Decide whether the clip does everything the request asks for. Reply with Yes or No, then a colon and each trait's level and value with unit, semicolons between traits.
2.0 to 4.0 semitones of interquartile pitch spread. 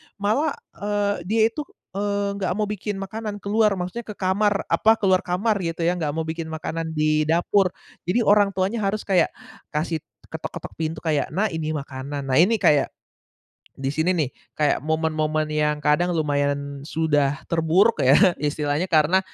No: average, 4.8 semitones